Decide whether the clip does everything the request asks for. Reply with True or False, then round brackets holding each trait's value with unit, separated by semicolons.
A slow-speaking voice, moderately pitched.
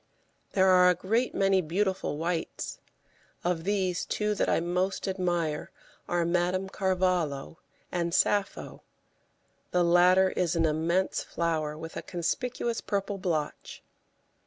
True (125 wpm; 180 Hz)